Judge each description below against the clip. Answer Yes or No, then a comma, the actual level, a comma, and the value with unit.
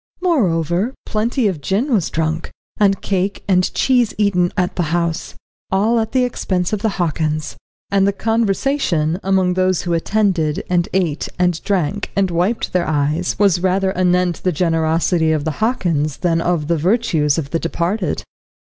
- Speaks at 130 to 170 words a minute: Yes, average, 165 wpm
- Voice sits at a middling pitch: Yes, medium, 180 Hz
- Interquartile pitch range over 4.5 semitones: No, average, 3.5 semitones